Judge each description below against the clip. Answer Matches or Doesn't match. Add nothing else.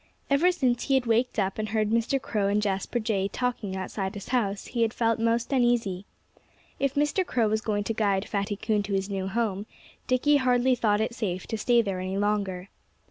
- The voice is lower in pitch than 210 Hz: Doesn't match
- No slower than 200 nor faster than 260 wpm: Matches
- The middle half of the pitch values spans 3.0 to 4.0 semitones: Matches